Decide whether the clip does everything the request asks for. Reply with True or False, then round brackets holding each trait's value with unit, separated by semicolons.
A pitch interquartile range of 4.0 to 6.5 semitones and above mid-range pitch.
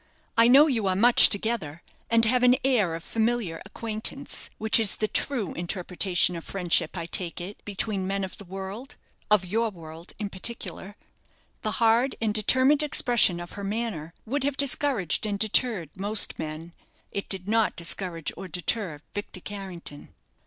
True (4.3 semitones; 205 Hz)